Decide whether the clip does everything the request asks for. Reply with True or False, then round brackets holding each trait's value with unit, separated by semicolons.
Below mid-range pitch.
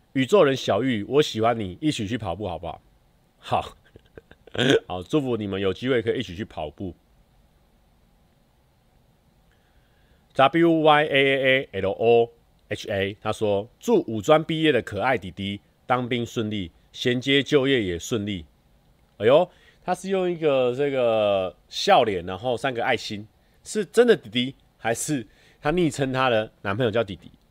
True (120 Hz)